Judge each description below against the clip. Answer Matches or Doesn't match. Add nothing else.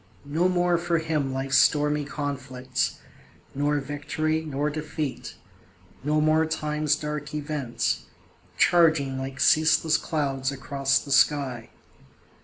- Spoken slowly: Matches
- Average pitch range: Doesn't match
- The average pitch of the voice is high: Doesn't match